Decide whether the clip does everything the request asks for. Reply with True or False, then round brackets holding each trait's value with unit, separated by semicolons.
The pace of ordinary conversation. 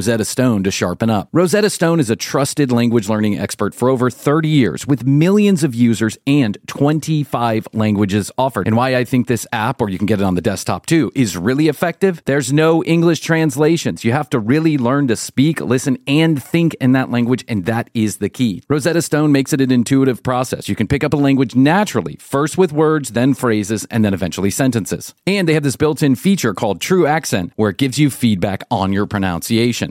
False (210 wpm)